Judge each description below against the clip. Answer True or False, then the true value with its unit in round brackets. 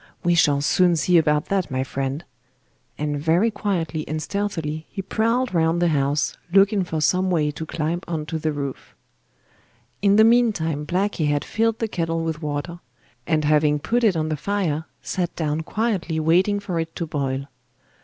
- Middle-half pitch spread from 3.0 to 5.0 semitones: True (4.2 semitones)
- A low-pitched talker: False (165 Hz)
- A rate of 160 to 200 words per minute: True (175 wpm)